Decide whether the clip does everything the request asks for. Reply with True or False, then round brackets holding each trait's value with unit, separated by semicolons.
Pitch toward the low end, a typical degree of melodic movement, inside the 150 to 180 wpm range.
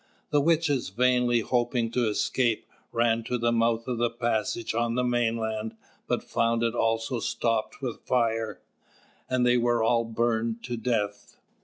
False (115 Hz; 1.3 semitones; 155 wpm)